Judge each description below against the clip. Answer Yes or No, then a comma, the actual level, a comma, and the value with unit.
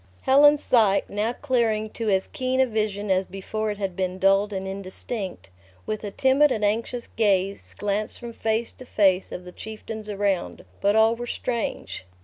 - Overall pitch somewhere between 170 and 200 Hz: No, high, 215 Hz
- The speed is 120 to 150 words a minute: No, average, 175 wpm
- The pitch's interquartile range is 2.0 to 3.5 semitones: Yes, average, 3.0 semitones